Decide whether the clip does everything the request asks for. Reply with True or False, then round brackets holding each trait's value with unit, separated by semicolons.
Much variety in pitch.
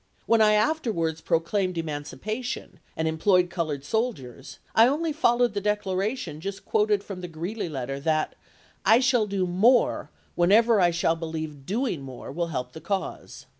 True (5.7 semitones)